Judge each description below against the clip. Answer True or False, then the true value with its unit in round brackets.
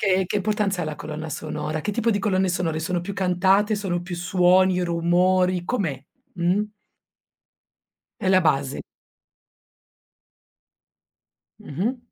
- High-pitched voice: False (180 Hz)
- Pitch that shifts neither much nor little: False (2.3 semitones)